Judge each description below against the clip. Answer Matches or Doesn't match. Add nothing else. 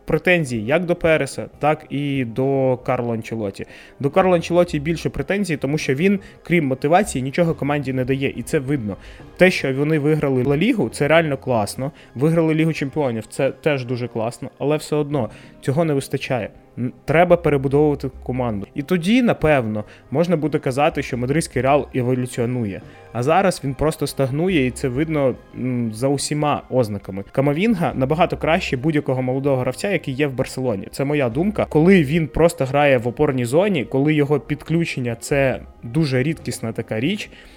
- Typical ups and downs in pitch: Matches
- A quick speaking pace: Matches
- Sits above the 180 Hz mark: Doesn't match